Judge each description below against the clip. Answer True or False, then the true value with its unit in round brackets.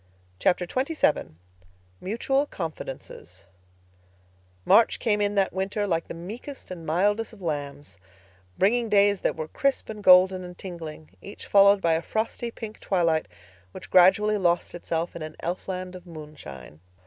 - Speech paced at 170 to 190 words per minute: False (145 wpm)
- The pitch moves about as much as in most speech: True (4.1 semitones)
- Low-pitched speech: False (185 Hz)